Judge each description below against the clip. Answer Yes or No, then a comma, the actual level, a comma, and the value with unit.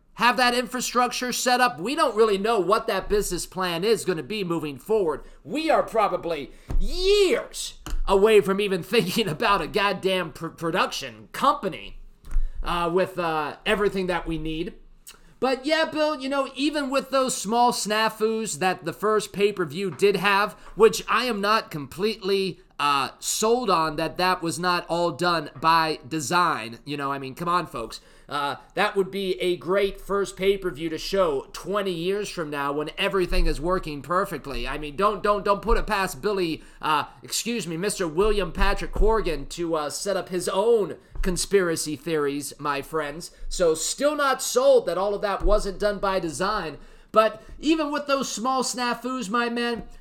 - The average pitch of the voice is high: Yes, high, 195 Hz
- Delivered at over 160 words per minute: Yes, average, 175 wpm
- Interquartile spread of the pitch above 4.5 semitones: Yes, average, 4.9 semitones